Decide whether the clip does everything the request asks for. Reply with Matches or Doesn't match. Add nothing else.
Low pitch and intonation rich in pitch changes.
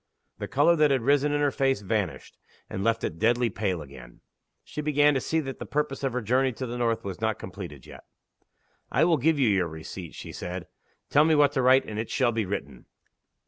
Matches